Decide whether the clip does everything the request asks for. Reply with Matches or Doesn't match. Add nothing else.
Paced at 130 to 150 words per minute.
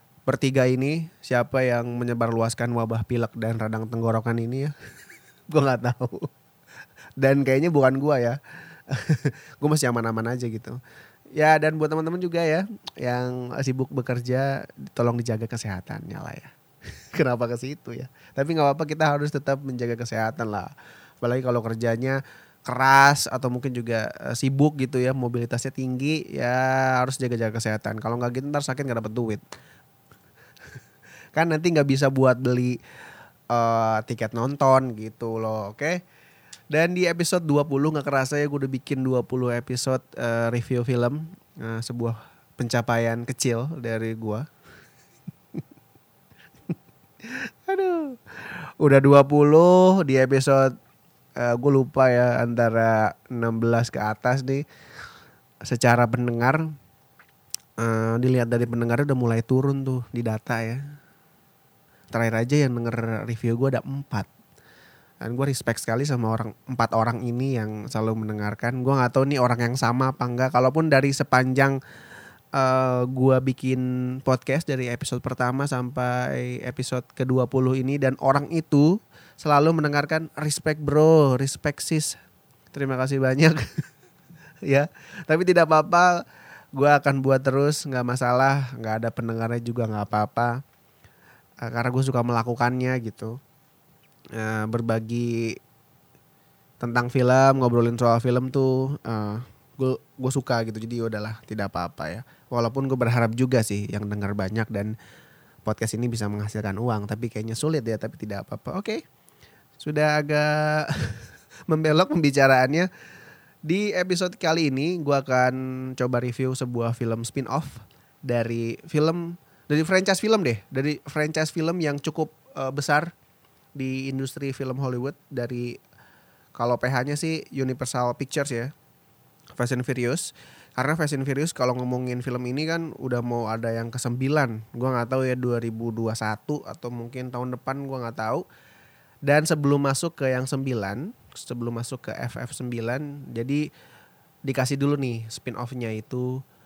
Matches